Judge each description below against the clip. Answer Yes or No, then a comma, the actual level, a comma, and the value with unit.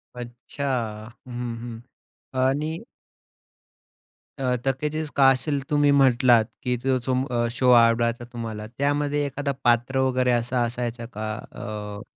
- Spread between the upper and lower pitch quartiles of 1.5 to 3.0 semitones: Yes, narrow, 2.5 semitones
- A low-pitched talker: Yes, low, 125 Hz